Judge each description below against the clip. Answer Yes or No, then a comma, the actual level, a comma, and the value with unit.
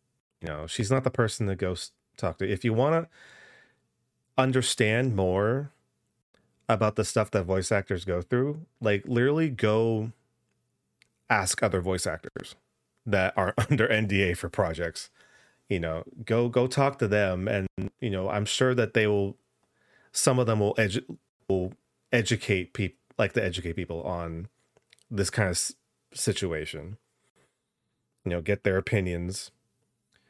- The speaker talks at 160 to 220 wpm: No, average, 145 wpm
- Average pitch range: Yes, average, 4.2 semitones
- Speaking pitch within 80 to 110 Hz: Yes, low, 105 Hz